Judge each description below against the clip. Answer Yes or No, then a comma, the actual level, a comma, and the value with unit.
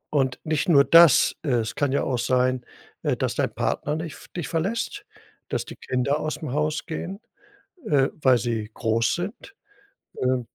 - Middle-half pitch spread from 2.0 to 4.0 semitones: No, average, 4.4 semitones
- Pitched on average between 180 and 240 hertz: No, medium, 140 Hz